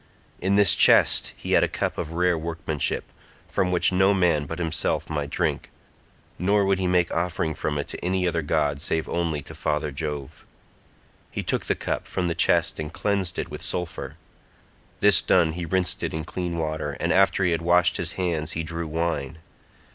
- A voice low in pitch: Yes, very low, 85 Hz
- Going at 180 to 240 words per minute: Yes, average, 190 wpm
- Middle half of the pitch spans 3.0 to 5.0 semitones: No, narrow, 2.5 semitones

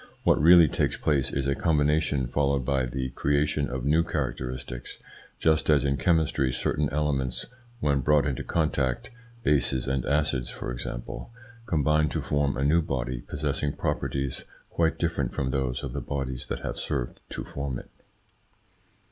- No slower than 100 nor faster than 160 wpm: Yes, average, 155 wpm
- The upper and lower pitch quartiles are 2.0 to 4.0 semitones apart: Yes, narrow, 2.6 semitones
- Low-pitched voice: Yes, very low, 70 Hz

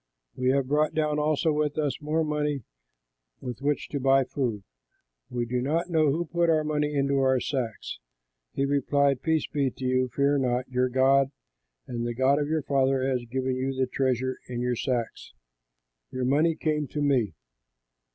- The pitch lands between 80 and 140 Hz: Yes, low, 135 Hz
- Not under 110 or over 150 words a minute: No, average, 175 wpm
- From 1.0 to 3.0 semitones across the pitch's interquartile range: Yes, narrow, 2.6 semitones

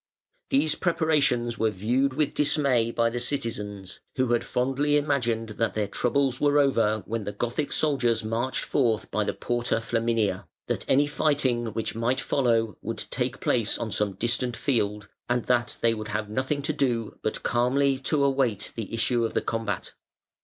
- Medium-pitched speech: No, low, 120 Hz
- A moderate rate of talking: Yes, average, 170 wpm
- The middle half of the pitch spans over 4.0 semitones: No, average, 3.4 semitones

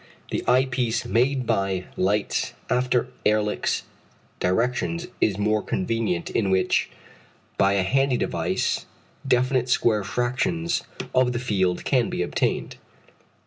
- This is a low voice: Yes, low, 115 Hz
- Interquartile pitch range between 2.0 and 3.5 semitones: No, average, 4.1 semitones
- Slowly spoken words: Yes, slow, 120 wpm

